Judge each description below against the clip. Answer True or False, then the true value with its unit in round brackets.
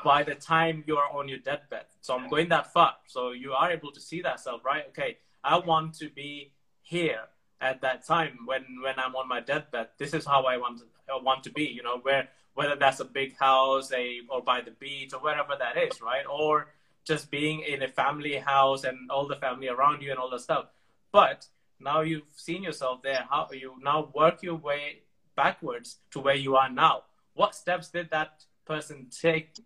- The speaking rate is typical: False (215 wpm)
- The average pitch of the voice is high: False (140 Hz)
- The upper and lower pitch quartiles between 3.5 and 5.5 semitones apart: False (2.9 semitones)